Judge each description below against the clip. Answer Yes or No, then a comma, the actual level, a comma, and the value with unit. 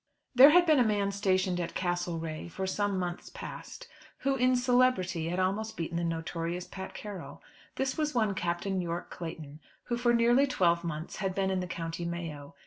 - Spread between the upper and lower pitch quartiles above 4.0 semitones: Yes, wide, 5.4 semitones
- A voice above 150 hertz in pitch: Yes, medium, 185 Hz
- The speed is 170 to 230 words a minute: Yes, average, 185 wpm